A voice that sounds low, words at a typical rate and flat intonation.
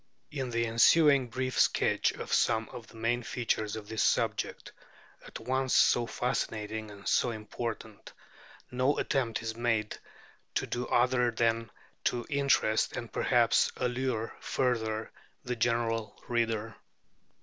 No: low, 115 Hz; slow, 130 wpm; narrow, 1.9 semitones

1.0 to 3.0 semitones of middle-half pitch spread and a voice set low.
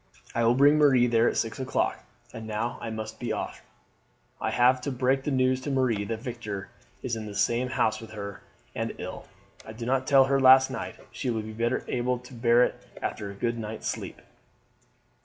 Yes: average, 2.7 semitones; low, 120 Hz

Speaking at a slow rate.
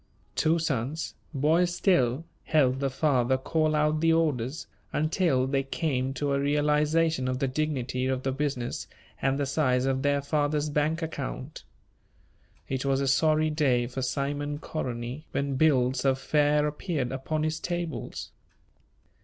No: average, 145 wpm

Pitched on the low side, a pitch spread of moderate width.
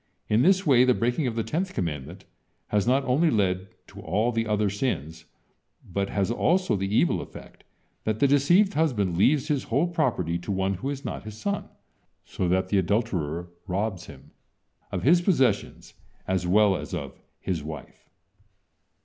No: low, 105 Hz; wide, 6.6 semitones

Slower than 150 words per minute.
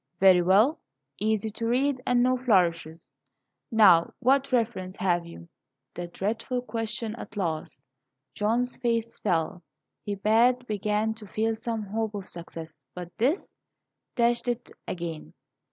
Yes: slow, 135 wpm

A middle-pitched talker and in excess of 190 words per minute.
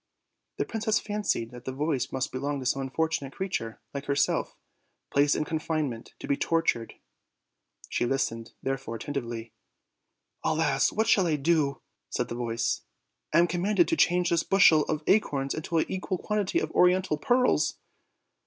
No: medium, 150 Hz; average, 155 wpm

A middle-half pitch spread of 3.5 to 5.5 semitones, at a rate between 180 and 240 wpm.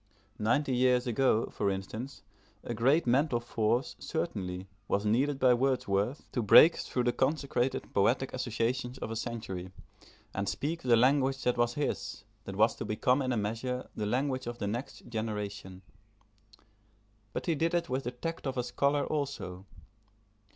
No: average, 3.9 semitones; average, 160 wpm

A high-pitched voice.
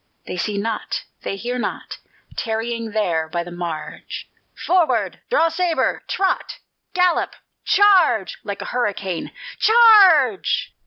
Yes: high, 230 Hz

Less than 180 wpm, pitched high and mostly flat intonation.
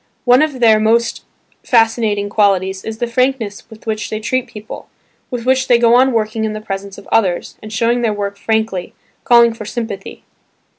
No: average, 185 wpm; high, 220 Hz; narrow, 2.3 semitones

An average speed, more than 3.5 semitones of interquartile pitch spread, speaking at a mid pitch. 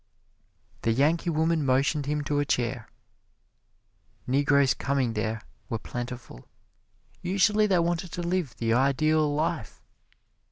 No: slow, 120 wpm; average, 4.9 semitones; medium, 145 Hz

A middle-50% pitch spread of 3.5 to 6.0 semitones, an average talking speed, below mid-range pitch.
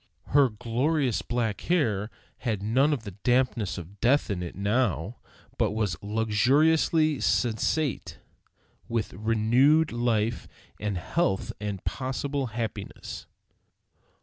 No: average, 4.3 semitones; slow, 105 wpm; low, 115 Hz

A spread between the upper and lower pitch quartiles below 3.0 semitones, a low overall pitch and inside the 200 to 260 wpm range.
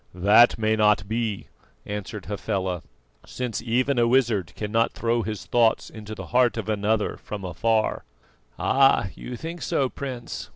No: narrow, 2.5 semitones; low, 110 Hz; average, 150 wpm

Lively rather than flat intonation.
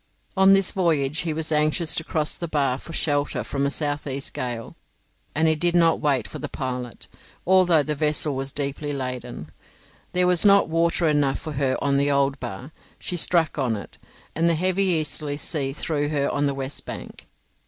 No: average, 3.2 semitones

